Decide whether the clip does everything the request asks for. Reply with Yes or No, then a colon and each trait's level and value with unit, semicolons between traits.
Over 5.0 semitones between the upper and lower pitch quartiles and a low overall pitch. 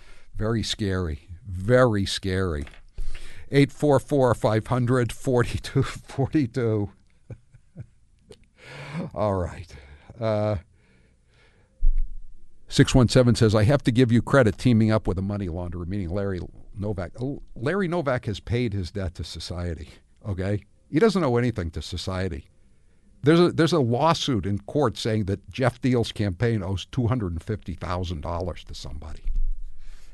Yes: wide, 5.5 semitones; low, 105 Hz